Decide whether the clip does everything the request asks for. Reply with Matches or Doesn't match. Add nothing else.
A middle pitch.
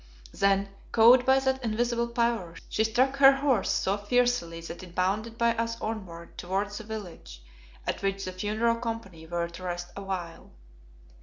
Doesn't match